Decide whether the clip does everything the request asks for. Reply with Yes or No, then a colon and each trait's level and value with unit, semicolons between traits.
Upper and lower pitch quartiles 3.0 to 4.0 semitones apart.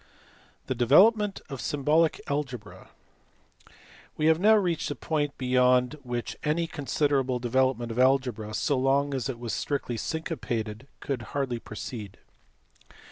Yes: average, 3.6 semitones